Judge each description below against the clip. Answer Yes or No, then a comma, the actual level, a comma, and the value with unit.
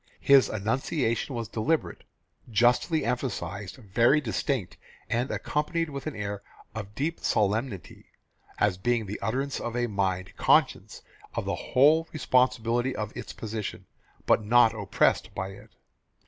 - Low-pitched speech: Yes, low, 115 Hz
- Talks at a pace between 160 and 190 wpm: No, slow, 135 wpm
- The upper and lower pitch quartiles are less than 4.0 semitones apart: No, average, 4.3 semitones